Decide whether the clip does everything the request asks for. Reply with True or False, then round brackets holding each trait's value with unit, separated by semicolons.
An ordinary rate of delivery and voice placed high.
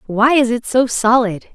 True (195 wpm; 240 Hz)